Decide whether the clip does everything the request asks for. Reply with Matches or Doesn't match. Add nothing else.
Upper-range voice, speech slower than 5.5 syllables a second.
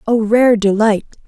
Matches